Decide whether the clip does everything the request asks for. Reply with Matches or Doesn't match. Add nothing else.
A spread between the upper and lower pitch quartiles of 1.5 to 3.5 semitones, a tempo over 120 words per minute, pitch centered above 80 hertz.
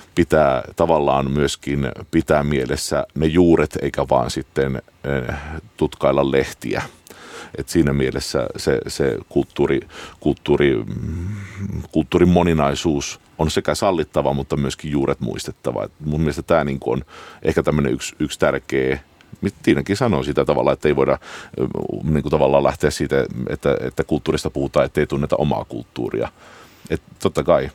Doesn't match